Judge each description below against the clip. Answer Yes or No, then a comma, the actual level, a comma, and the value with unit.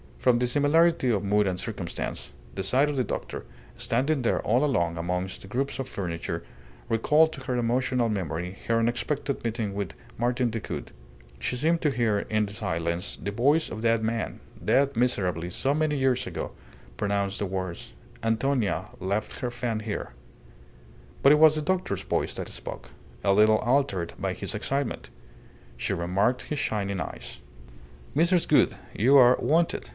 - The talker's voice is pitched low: Yes, low, 115 Hz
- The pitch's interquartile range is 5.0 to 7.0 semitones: Yes, wide, 5.4 semitones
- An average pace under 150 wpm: No, average, 165 wpm